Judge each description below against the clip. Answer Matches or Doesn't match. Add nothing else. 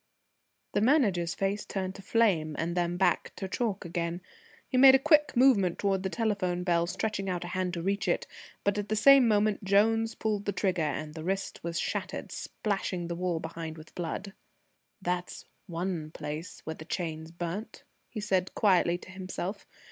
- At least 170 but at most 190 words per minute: Matches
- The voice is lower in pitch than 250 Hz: Matches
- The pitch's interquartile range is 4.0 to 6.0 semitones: Doesn't match